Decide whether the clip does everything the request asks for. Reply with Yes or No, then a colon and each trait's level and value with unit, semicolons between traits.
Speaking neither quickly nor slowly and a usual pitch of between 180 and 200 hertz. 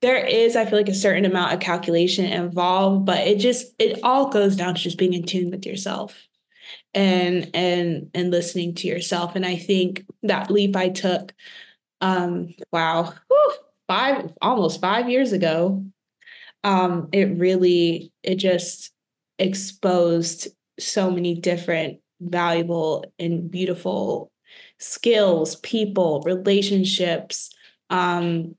No: slow, 130 wpm; medium, 185 Hz